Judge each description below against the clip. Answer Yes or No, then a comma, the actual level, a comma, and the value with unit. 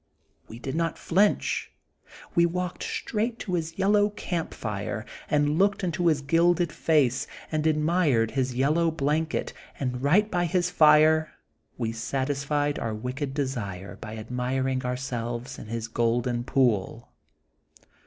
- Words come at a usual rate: No, slow, 130 wpm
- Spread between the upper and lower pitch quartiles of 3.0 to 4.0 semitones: No, average, 5.2 semitones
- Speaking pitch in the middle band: Yes, medium, 145 Hz